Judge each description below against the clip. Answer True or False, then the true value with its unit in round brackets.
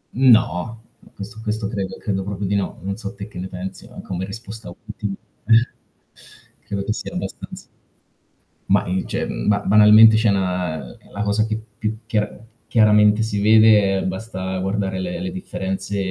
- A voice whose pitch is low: True (105 Hz)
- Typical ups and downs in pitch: False (2.3 semitones)